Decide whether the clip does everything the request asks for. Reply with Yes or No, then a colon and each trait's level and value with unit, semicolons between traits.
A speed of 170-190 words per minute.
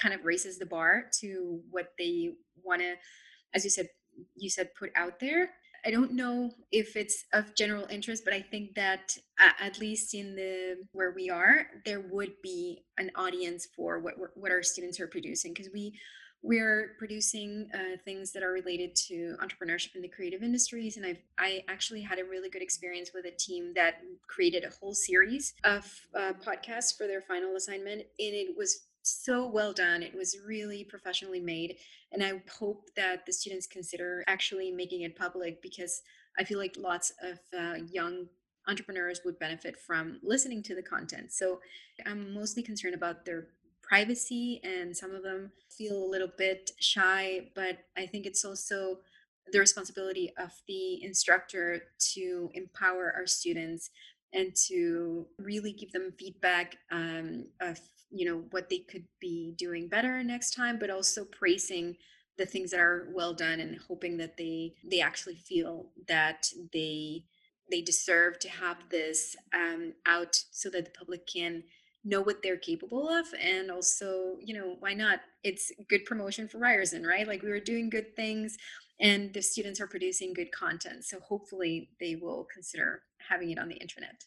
Yes: average, 175 wpm